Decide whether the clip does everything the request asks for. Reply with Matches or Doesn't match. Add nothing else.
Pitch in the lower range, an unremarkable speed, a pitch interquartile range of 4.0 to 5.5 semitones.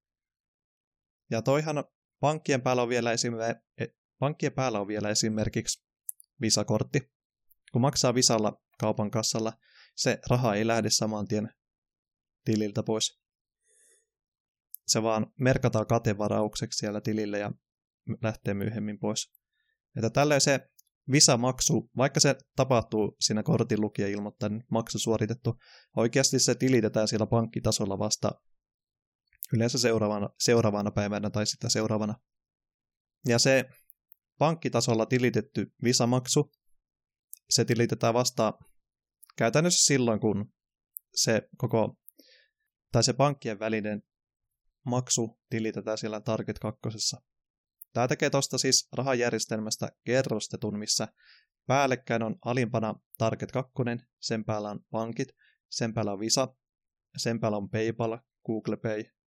Doesn't match